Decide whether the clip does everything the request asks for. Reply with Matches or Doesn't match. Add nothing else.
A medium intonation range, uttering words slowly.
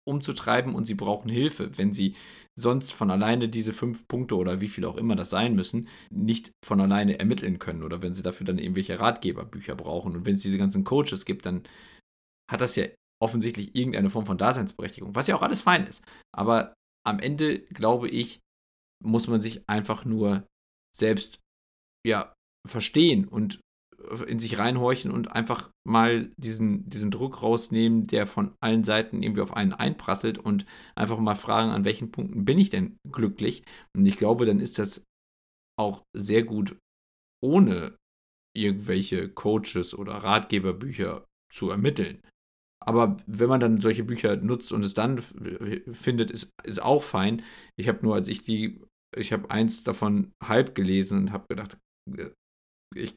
Doesn't match